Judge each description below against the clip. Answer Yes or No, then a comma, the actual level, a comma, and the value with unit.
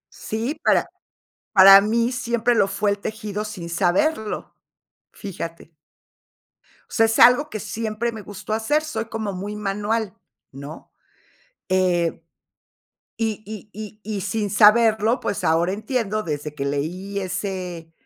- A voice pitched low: No, high, 210 Hz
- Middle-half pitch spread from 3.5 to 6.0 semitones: No, average, 3.1 semitones